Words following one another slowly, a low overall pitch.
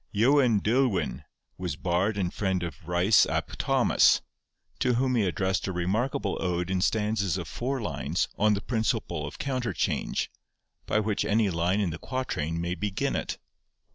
No: average, 165 wpm; low, 100 Hz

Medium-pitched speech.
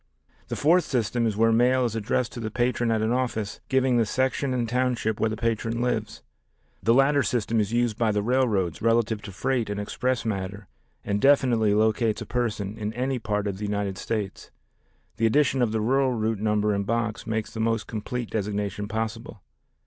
No: low, 115 Hz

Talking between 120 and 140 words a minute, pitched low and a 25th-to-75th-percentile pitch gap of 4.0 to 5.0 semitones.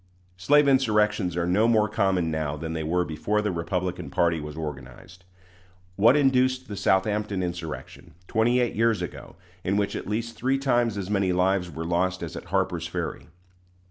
No: average, 175 wpm; very low, 95 Hz; average, 4.4 semitones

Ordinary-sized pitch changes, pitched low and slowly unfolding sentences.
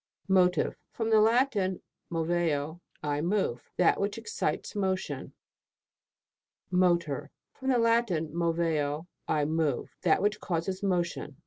No: average, 4.2 semitones; medium, 175 Hz; slow, 115 wpm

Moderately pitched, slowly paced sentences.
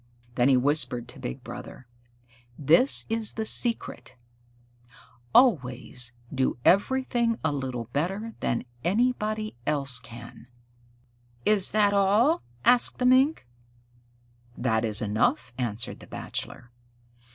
Yes: medium, 155 Hz; slow, 115 wpm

